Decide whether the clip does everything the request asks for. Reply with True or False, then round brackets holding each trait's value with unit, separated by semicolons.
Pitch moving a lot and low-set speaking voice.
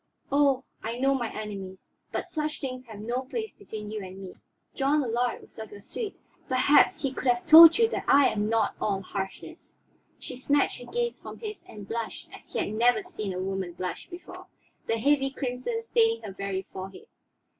False (6.3 semitones; 250 Hz)